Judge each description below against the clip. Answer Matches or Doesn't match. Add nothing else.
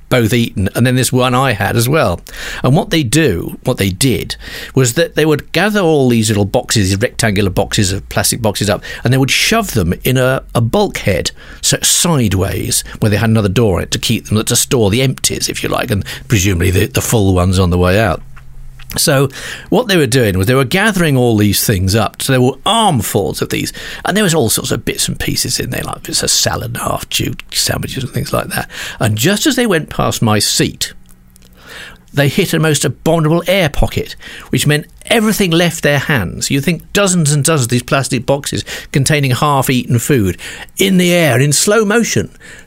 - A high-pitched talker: Doesn't match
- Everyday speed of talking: Doesn't match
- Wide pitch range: Matches